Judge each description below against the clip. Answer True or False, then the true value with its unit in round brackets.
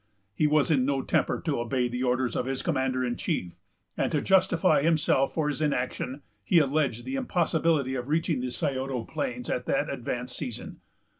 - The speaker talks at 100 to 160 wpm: False (180 wpm)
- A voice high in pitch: False (135 Hz)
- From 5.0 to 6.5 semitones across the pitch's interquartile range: False (3.7 semitones)